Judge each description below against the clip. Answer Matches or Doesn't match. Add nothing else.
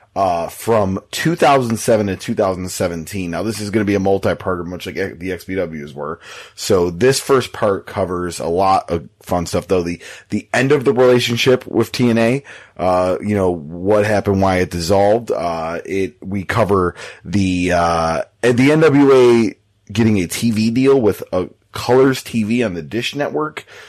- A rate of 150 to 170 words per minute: Matches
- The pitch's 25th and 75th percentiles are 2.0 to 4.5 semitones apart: Doesn't match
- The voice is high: Doesn't match